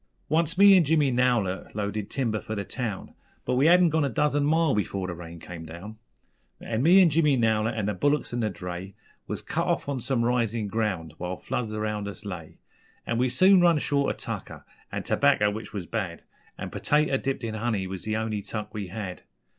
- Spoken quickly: Yes, fast, 210 wpm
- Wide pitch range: Yes, wide, 5.7 semitones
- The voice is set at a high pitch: No, low, 110 Hz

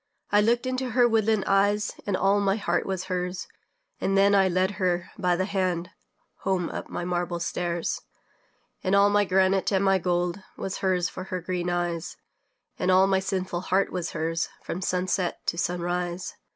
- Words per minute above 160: Yes, average, 180 wpm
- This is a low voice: No, medium, 185 Hz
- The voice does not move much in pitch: Yes, narrow, 1.9 semitones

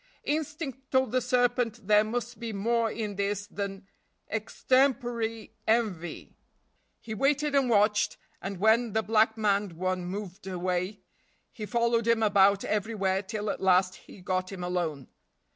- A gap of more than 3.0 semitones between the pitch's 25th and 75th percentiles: Yes, average, 3.4 semitones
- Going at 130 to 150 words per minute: Yes, average, 145 wpm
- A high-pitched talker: Yes, high, 215 Hz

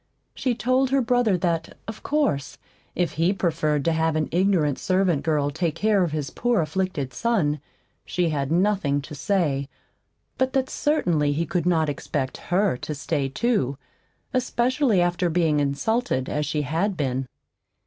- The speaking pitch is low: No, medium, 170 Hz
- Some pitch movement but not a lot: No, wide, 5.9 semitones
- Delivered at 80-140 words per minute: No, average, 160 wpm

